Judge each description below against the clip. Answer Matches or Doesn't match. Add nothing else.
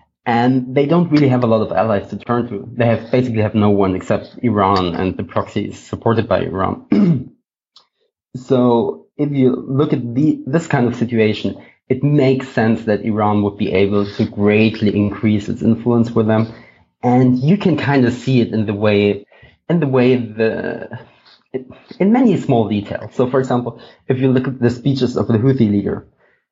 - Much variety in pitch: Doesn't match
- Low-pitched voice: Matches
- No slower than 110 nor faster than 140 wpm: Doesn't match